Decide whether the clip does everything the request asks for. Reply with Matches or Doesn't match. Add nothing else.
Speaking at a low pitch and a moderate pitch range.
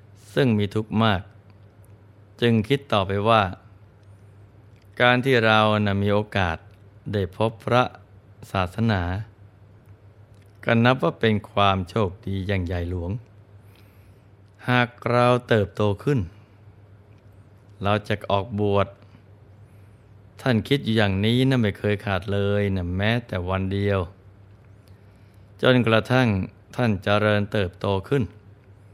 Doesn't match